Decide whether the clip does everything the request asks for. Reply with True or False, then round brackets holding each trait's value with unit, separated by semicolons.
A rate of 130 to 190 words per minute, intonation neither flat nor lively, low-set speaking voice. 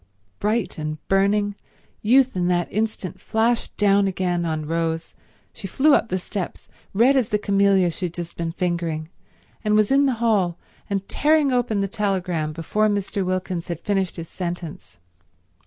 False (165 wpm; 3.7 semitones; 195 Hz)